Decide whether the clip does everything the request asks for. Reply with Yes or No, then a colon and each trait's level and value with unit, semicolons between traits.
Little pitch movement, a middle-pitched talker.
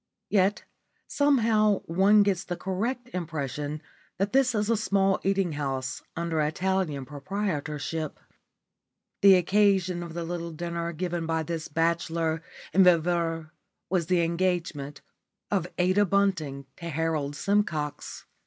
No: average, 3.6 semitones; medium, 170 Hz